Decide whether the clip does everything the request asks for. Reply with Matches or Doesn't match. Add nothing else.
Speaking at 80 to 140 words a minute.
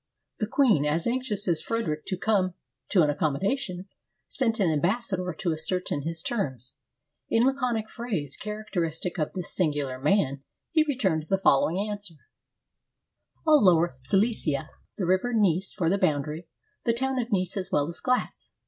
Doesn't match